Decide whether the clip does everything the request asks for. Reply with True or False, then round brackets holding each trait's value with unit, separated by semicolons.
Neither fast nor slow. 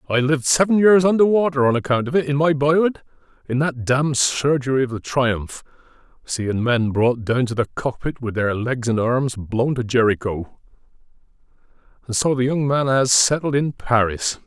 True (175 wpm)